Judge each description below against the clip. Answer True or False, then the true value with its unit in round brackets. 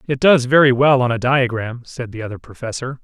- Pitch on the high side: False (125 Hz)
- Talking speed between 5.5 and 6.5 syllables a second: True (5.6 syllables/s)